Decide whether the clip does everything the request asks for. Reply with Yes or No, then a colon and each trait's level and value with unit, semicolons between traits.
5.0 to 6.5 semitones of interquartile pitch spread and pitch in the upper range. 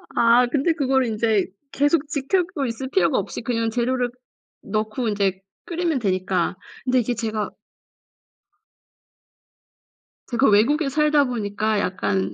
No: average, 4.5 semitones; high, 240 Hz